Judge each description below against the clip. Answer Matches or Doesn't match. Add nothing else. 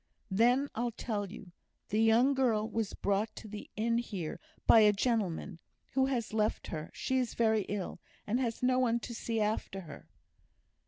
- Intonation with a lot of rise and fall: Doesn't match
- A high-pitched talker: Matches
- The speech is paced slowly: Doesn't match